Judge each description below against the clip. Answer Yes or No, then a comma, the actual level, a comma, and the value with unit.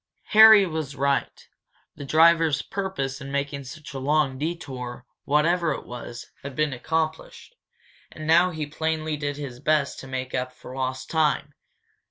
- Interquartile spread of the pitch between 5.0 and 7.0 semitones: No, average, 3.1 semitones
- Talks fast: No, average, 155 wpm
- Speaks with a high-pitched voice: No, medium, 145 Hz